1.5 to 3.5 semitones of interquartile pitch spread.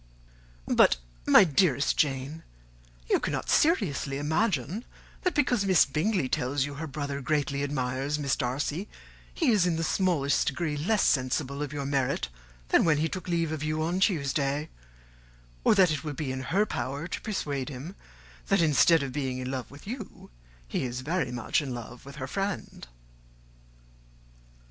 No: average, 4.3 semitones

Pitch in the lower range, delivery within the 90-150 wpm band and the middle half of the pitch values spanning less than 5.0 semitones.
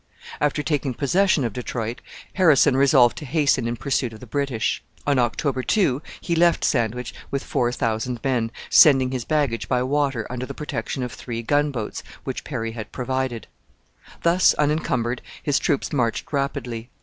No: low, 130 Hz; average, 160 wpm; average, 3.4 semitones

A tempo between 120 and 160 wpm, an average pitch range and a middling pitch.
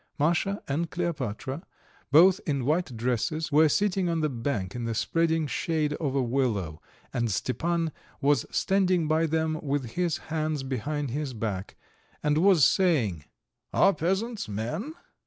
Yes: average, 145 wpm; average, 4.8 semitones; medium, 150 Hz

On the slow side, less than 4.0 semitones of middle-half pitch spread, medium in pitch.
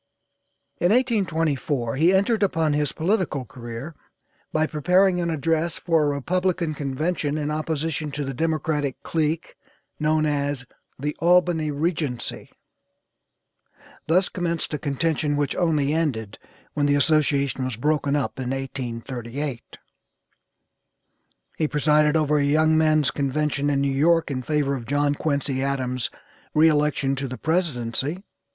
Yes: slow, 130 wpm; average, 2.8 semitones; medium, 150 Hz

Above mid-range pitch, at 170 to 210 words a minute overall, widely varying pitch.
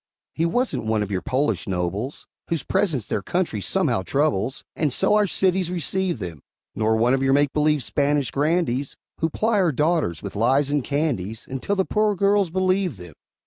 No: medium, 145 Hz; average, 185 wpm; wide, 8.1 semitones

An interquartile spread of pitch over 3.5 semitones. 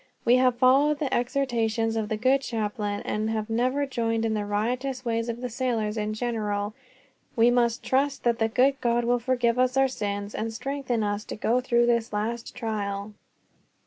No: narrow, 2.6 semitones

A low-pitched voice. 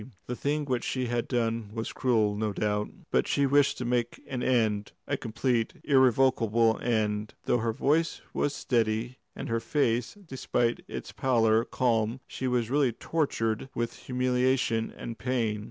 Yes: low, 120 Hz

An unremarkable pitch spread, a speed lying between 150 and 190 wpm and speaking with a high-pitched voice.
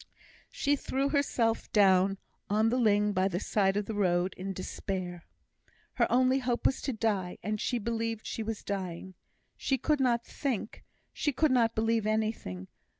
Yes: average, 4.0 semitones; average, 160 wpm; high, 215 Hz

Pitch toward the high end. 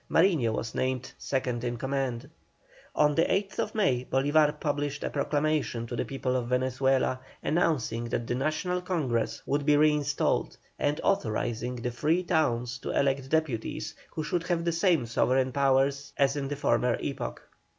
No: low, 135 Hz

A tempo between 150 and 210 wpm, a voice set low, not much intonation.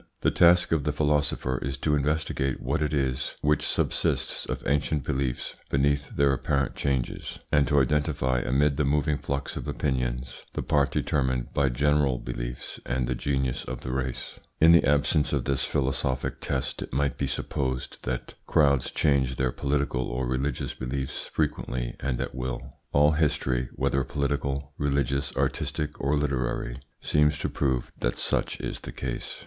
Yes: average, 165 wpm; very low, 70 Hz; narrow, 2.3 semitones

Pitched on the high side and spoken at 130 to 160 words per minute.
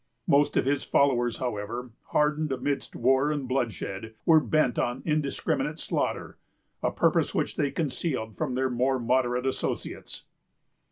No: low, 130 Hz; slow, 135 wpm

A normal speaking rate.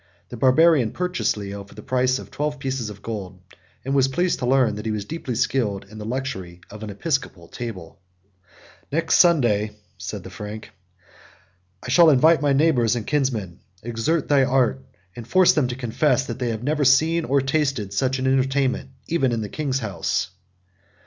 Yes: average, 180 wpm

